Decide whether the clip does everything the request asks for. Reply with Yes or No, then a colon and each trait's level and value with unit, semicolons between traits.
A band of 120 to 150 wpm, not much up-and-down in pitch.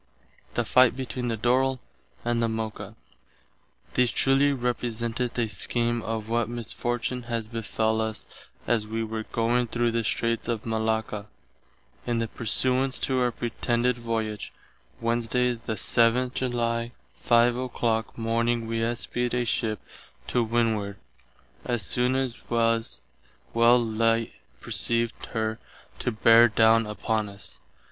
Yes: slow, 135 wpm; narrow, 1.4 semitones